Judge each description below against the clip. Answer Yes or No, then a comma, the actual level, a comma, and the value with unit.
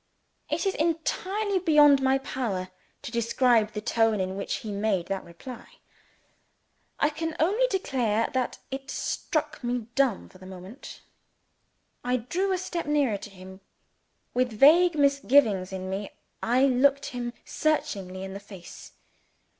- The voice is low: No, very high, 250 Hz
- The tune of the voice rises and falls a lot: Yes, wide, 6.5 semitones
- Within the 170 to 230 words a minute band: No, average, 145 wpm